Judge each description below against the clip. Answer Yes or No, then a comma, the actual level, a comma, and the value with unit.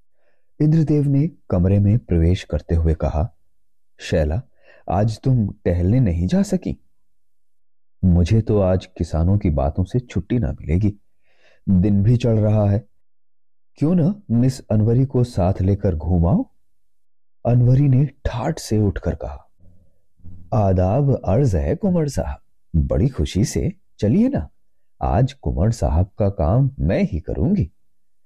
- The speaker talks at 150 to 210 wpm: No, average, 135 wpm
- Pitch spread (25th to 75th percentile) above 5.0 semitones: Yes, wide, 5.6 semitones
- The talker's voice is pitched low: Yes, low, 100 Hz